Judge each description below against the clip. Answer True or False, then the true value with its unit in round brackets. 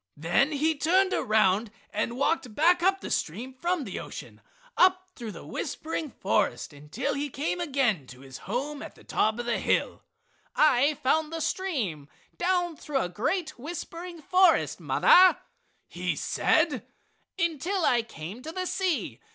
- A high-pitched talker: True (290 Hz)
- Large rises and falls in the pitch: True (7.3 semitones)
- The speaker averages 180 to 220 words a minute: False (155 wpm)